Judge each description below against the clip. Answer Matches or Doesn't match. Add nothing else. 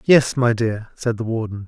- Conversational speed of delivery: Doesn't match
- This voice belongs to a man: Matches